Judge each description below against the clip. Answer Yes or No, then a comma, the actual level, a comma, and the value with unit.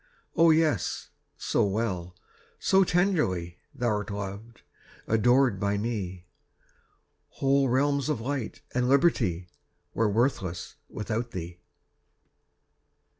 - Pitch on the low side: Yes, low, 115 Hz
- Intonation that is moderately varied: No, wide, 6.1 semitones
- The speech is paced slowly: Yes, slow, 95 wpm